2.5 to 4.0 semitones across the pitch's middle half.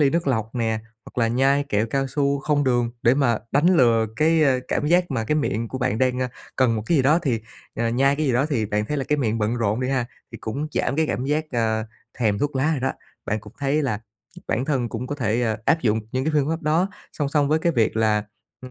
No: average, 4.4 semitones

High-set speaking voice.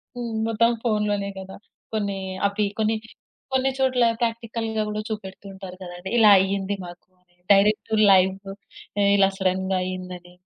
Yes: high, 200 Hz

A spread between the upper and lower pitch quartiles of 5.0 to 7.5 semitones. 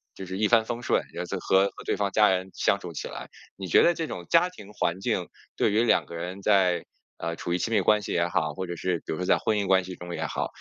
No: average, 3.2 semitones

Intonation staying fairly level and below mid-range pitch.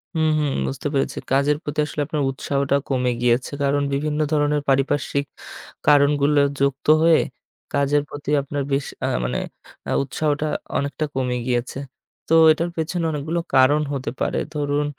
No: narrow, 1.4 semitones; medium, 145 Hz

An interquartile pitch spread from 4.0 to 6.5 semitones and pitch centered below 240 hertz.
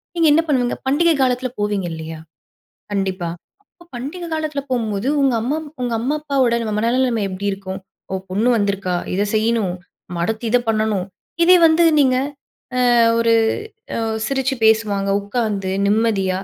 Yes: average, 4.7 semitones; high, 225 Hz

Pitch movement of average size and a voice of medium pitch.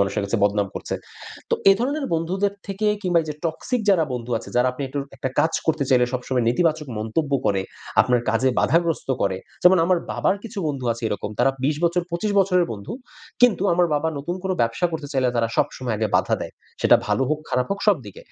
No: wide, 6.5 semitones; medium, 150 Hz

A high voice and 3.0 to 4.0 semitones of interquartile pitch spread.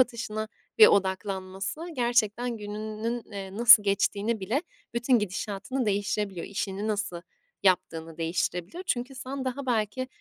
Yes: high, 210 Hz; average, 3.7 semitones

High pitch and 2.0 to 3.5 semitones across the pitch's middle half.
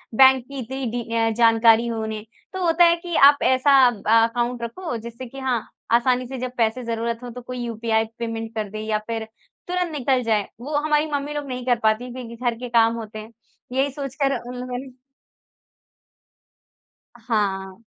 Yes: high, 240 Hz; average, 2.8 semitones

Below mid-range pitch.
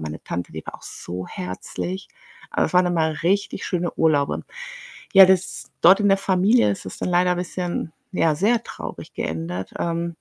No: medium, 175 Hz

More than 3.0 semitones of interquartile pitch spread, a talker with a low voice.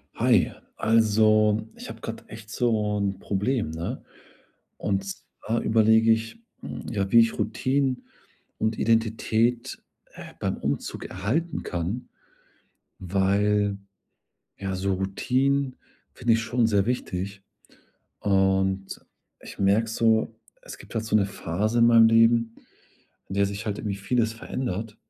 No: narrow, 2.6 semitones; low, 110 Hz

